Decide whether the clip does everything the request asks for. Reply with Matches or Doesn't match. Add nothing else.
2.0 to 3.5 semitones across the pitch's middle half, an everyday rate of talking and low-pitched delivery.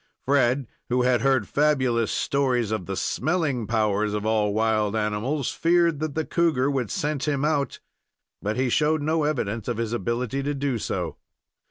Doesn't match